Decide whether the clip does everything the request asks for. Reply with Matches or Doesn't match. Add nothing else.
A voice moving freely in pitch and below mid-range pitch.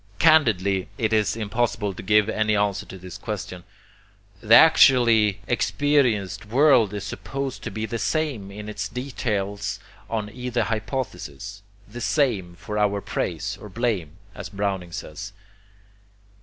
Doesn't match